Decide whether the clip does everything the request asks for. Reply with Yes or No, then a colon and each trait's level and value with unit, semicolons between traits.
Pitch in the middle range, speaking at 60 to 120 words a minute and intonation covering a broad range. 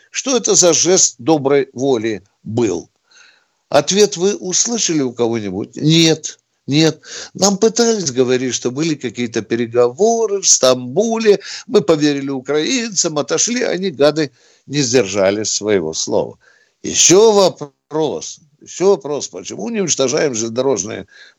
Yes: medium, 155 Hz; average, 115 wpm; wide, 7.4 semitones